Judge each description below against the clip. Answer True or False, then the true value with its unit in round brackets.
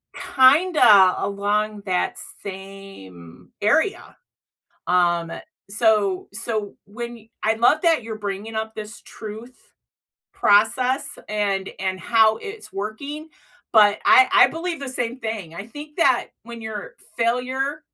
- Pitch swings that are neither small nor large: True (4.1 semitones)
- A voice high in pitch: True (220 Hz)